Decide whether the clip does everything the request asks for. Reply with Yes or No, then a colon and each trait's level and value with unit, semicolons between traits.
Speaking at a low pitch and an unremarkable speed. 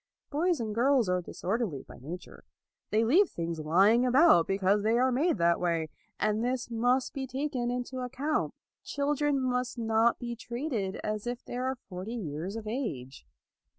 No: high, 235 Hz; average, 175 wpm